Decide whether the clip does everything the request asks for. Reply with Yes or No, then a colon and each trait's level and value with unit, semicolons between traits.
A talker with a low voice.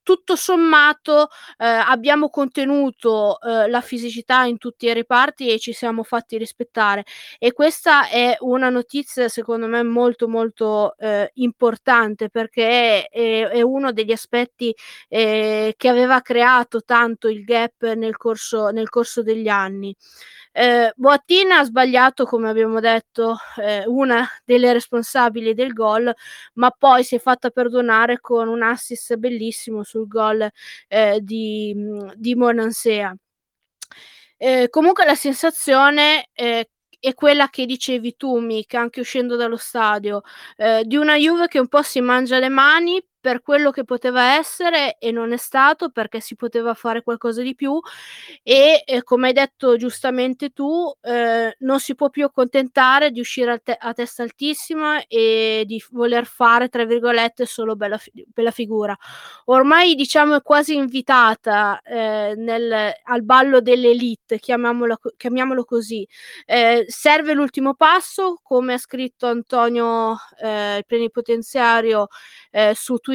No: high, 240 Hz